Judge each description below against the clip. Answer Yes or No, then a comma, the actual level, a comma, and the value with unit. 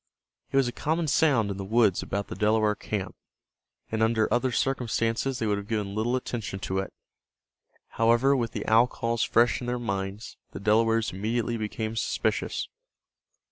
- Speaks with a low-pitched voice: Yes, low, 115 Hz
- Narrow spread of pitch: Yes, narrow, 2.3 semitones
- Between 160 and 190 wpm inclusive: Yes, average, 170 wpm